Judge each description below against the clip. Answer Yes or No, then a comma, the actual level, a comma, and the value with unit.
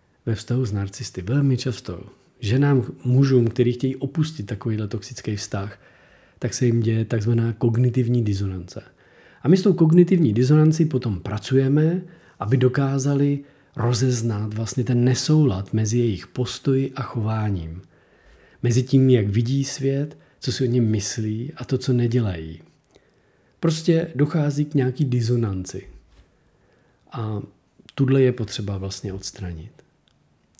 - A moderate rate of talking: Yes, average, 130 wpm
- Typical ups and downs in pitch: Yes, average, 4.0 semitones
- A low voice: Yes, low, 125 Hz